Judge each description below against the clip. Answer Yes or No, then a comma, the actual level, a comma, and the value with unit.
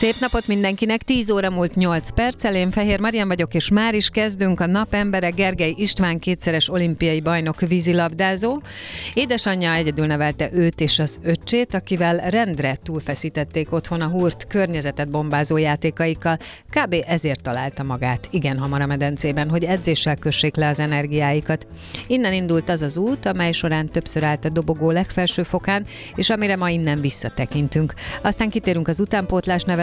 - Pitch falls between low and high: Yes, medium, 170 Hz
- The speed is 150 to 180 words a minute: Yes, fast, 155 wpm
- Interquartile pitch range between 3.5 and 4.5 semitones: Yes, average, 3.9 semitones